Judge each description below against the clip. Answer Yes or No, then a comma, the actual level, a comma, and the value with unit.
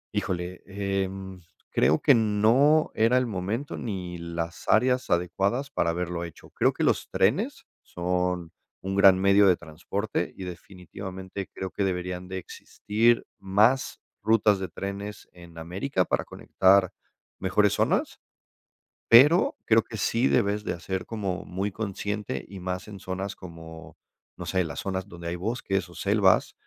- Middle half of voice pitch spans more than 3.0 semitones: No, average, 2.7 semitones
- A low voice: Yes, very low, 95 Hz